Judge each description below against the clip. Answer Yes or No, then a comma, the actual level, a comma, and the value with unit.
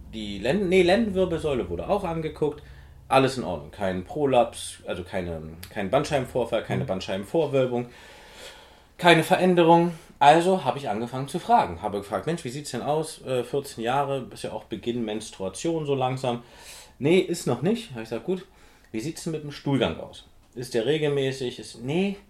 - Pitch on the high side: No, medium, 140 Hz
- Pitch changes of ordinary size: No, wide, 6.4 semitones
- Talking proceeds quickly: No, average, 175 wpm